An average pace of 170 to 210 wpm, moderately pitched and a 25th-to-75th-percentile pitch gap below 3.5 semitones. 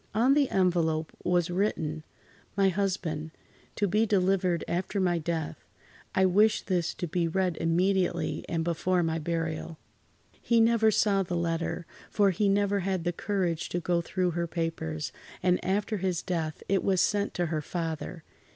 No: average, 160 wpm; medium, 180 Hz; average, 2.8 semitones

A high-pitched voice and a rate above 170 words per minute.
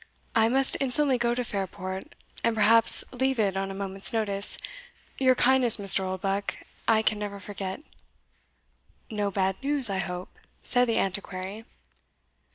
No: high, 210 Hz; average, 145 wpm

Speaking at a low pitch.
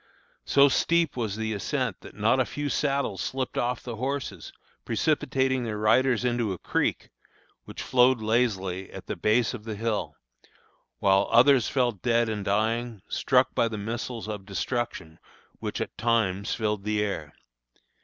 Yes: low, 115 Hz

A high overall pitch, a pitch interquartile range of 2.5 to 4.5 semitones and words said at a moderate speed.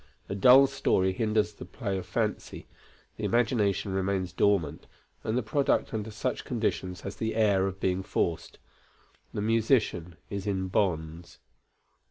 No: low, 100 Hz; average, 2.9 semitones; average, 145 wpm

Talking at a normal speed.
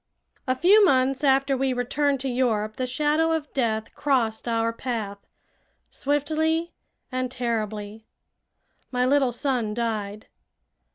No: slow, 120 wpm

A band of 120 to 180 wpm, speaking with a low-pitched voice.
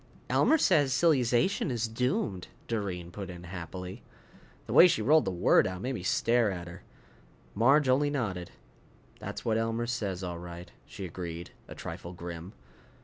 Yes: average, 165 wpm; low, 100 Hz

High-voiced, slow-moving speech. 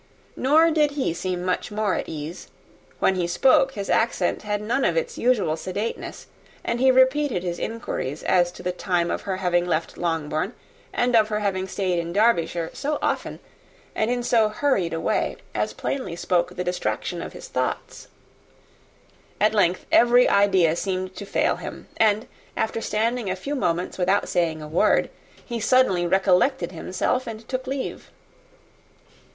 No: high, 200 Hz; average, 165 wpm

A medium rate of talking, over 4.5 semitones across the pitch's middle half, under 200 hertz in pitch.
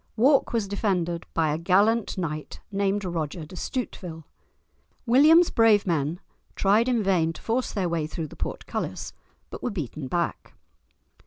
Yes: average, 150 wpm; average, 5.3 semitones; high, 190 Hz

